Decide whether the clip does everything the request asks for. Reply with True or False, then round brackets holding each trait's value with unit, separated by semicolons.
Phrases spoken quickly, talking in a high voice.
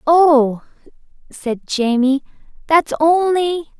False (80 wpm; 295 Hz)